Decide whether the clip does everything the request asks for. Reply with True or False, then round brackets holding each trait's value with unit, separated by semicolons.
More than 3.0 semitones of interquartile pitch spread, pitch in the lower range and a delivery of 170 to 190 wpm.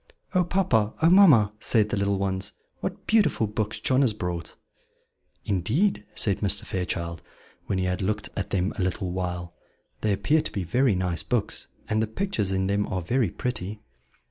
True (3.9 semitones; 100 Hz; 175 wpm)